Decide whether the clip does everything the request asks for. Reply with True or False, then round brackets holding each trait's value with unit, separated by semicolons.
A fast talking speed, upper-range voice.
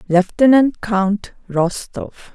False (75 wpm; 210 Hz)